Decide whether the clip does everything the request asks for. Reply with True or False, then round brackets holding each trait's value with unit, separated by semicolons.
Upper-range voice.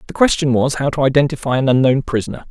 False (135 Hz)